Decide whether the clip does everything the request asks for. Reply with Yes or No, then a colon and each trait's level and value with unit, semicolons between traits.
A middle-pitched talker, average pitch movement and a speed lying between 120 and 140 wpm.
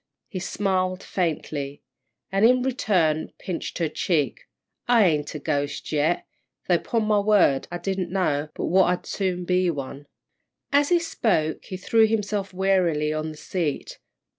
No: medium, 180 Hz; average, 4.5 semitones; average, 155 wpm